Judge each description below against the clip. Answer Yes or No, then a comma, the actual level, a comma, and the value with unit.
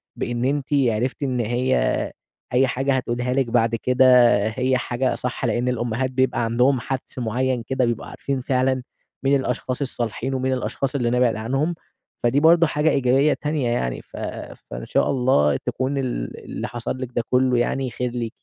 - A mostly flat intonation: Yes, narrow, 1.9 semitones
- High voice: No, low, 125 Hz